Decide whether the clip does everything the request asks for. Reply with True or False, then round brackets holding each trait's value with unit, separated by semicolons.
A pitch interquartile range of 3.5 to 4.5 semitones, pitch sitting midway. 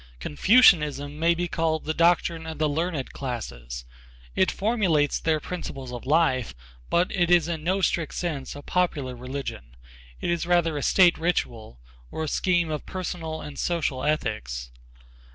True (4.1 semitones; 160 Hz)